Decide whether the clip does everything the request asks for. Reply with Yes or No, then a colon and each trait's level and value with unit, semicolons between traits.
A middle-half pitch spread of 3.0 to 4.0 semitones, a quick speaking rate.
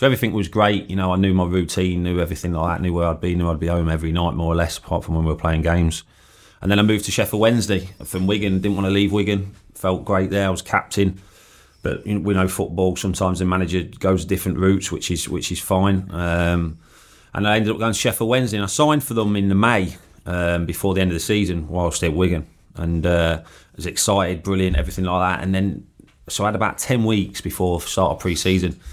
No: narrow, 2.5 semitones; fast, 250 wpm